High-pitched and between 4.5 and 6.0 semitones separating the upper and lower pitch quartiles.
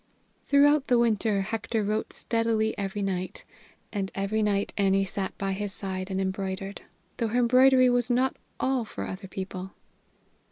No: high, 205 Hz; average, 3.5 semitones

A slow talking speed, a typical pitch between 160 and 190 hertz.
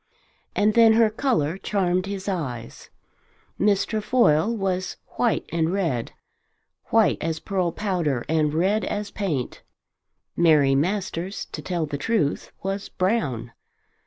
Yes: slow, 125 wpm; medium, 185 Hz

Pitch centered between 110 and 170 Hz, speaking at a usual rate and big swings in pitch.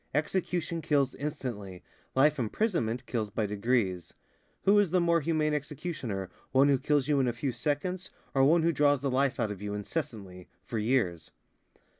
Yes: low, 135 Hz; average, 170 wpm; wide, 5.7 semitones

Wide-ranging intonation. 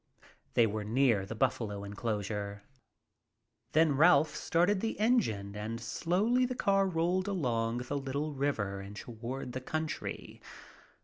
Yes: wide, 7.9 semitones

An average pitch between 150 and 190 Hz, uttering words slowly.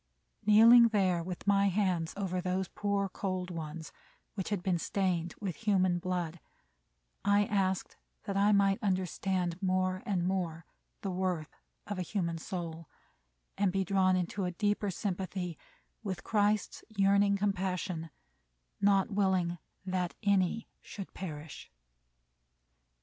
Yes: medium, 185 Hz; slow, 130 wpm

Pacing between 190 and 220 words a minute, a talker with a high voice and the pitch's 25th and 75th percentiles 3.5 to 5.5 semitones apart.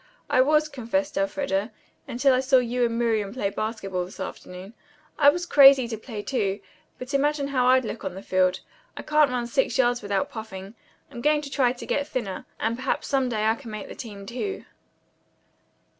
Yes: average, 195 wpm; high, 245 Hz; average, 4.6 semitones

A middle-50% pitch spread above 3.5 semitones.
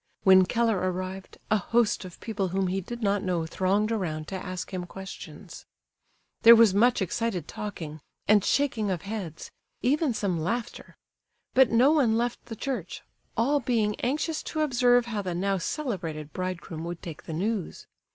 Yes: average, 4.3 semitones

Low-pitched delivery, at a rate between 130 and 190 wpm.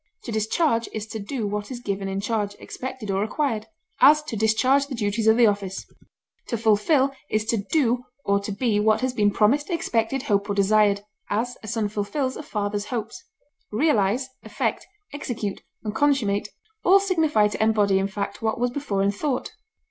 No: high, 220 Hz; average, 180 wpm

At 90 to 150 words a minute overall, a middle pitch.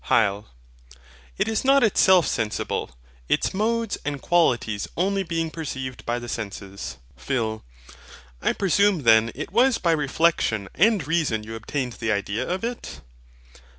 Yes: average, 140 wpm; medium, 145 Hz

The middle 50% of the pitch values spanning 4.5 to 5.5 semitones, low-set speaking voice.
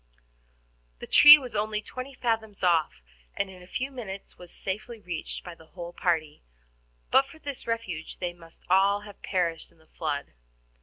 No: average, 5.0 semitones; high, 190 Hz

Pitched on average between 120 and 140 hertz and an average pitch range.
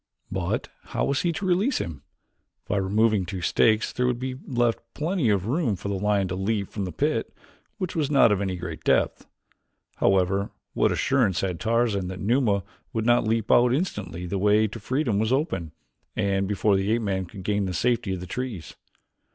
No: low, 105 Hz; average, 4.2 semitones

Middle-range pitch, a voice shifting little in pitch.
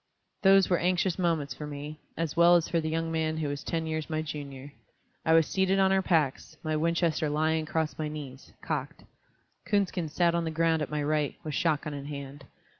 Yes: medium, 160 Hz; narrow, 2.1 semitones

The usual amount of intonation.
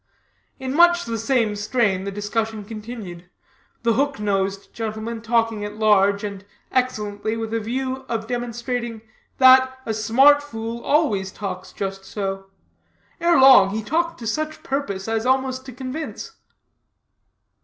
Yes: average, 4.0 semitones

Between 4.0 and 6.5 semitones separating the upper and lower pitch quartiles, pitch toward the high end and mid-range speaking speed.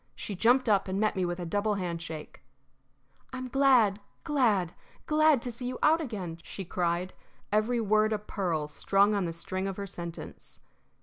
Yes: average, 5.1 semitones; high, 200 Hz; average, 175 wpm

